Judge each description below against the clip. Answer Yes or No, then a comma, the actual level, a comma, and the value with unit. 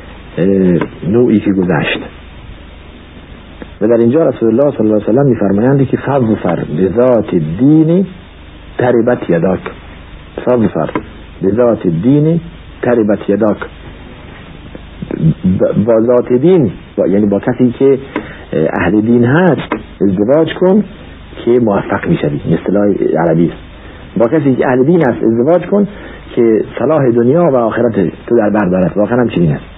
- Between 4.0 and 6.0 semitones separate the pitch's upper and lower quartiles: Yes, average, 5.1 semitones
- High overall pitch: No, low, 115 Hz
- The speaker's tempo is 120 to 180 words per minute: Yes, average, 135 wpm